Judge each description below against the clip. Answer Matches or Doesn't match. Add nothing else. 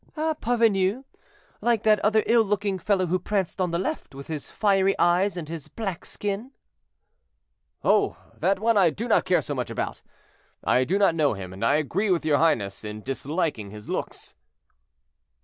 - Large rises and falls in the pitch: Matches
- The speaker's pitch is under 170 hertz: Doesn't match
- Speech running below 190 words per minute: Matches